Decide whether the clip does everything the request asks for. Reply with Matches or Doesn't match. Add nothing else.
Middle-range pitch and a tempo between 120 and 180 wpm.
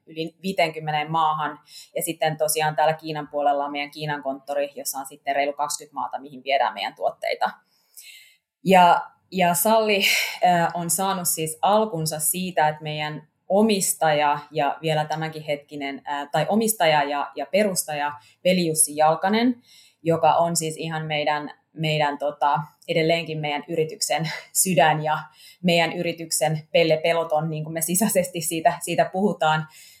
Matches